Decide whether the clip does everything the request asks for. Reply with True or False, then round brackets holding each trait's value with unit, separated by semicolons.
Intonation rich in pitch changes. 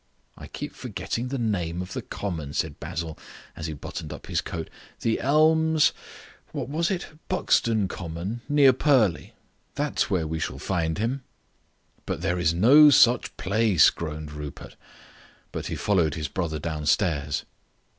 True (7.4 semitones)